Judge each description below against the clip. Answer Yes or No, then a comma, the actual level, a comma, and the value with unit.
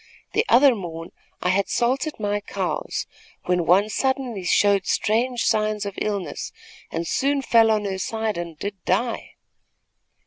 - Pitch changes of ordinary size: Yes, average, 4.0 semitones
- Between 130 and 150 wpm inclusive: Yes, average, 145 wpm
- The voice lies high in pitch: Yes, high, 210 Hz